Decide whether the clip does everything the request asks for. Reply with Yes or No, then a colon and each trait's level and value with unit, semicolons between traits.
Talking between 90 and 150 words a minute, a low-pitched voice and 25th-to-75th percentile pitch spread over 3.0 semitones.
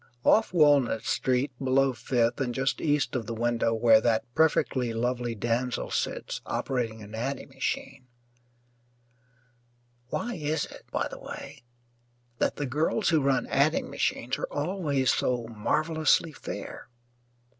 Yes: slow, 135 wpm; low, 130 Hz; average, 3.9 semitones